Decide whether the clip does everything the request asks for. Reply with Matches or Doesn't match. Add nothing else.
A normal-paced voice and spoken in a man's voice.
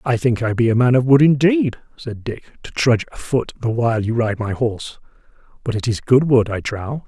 Doesn't match